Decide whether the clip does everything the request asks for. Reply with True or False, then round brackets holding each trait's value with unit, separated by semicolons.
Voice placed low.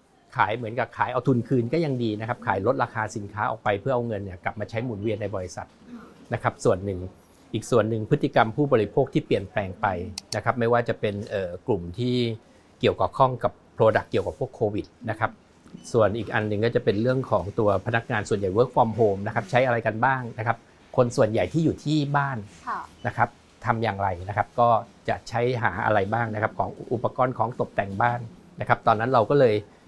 True (115 Hz)